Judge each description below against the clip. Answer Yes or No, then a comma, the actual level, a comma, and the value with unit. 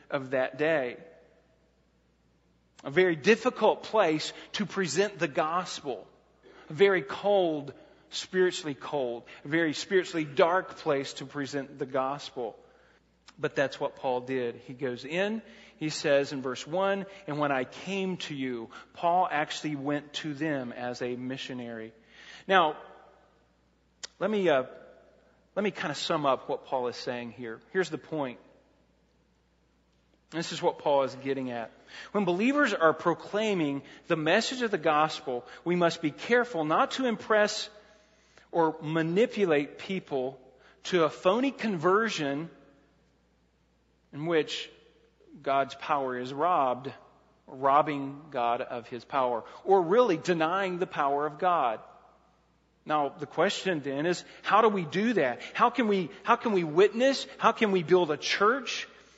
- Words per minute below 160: Yes, average, 145 wpm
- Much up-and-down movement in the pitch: Yes, wide, 5.8 semitones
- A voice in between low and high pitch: Yes, medium, 155 Hz